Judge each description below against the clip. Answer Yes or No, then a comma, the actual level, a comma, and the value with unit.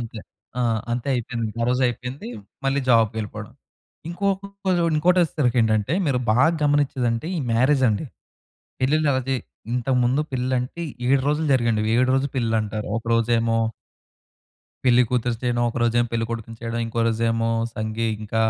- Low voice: Yes, low, 120 Hz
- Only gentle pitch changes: No, average, 3.0 semitones